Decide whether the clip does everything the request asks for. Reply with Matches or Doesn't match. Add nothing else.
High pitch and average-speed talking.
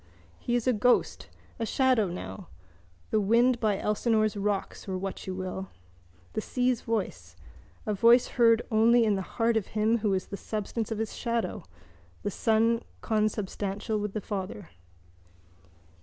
Matches